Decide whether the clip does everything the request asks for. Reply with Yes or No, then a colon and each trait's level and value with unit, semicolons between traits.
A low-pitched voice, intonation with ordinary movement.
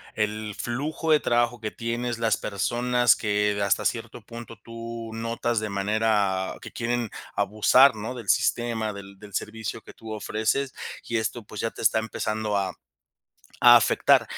No: low, 110 Hz; narrow, 2.1 semitones